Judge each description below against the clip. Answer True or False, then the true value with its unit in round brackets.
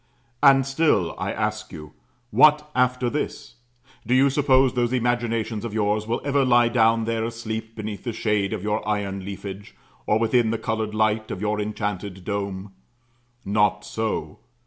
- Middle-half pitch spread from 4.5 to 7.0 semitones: False (2.7 semitones)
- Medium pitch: False (110 Hz)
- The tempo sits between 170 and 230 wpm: False (160 wpm)